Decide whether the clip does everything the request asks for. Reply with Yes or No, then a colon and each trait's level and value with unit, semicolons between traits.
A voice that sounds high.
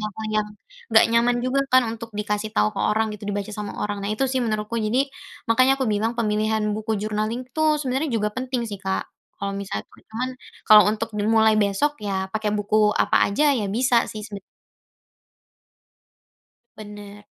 Yes: high, 215 Hz